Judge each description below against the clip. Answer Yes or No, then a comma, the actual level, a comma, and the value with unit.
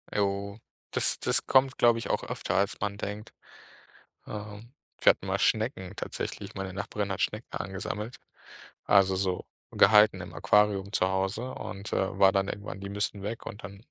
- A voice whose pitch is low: Yes, low, 100 Hz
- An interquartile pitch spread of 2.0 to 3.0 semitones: No, narrow, 1.5 semitones